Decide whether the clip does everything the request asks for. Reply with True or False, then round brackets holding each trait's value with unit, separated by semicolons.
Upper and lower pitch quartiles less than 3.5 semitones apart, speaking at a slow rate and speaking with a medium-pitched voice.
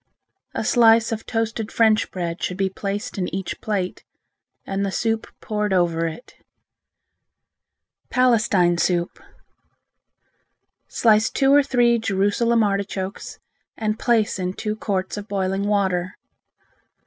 False (3.1 semitones; 120 wpm; 205 Hz)